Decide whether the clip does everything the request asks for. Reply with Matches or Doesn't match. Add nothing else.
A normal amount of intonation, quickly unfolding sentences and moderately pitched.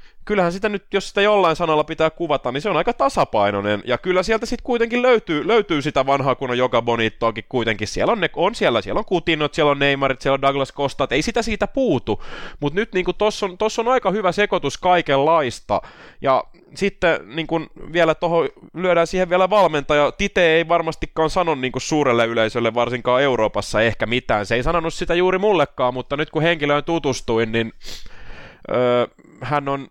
Doesn't match